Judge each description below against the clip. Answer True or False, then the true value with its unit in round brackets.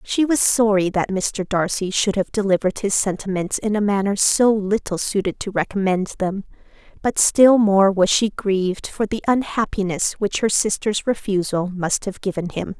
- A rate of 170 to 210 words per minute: True (175 wpm)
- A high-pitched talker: True (200 Hz)